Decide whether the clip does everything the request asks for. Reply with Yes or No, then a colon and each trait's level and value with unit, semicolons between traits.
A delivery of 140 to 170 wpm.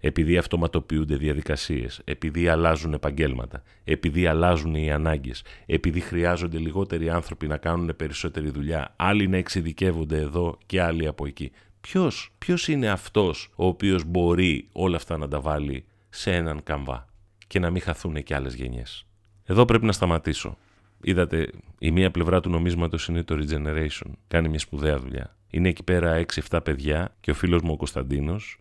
Yes: average, 155 wpm